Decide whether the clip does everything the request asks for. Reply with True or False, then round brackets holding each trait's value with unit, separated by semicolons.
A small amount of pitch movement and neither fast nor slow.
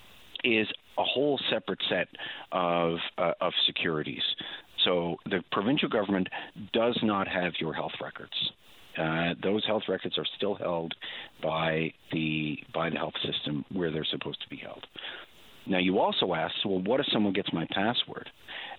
True (2.1 semitones; 160 wpm)